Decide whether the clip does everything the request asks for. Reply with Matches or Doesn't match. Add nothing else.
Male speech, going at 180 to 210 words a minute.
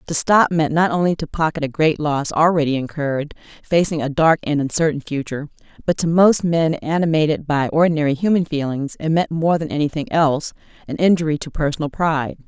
Doesn't match